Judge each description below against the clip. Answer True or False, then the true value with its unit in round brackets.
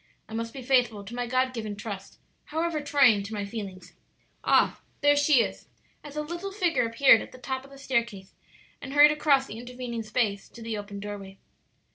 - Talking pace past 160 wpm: True (195 wpm)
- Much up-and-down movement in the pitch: False (4.8 semitones)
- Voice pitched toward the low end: False (245 Hz)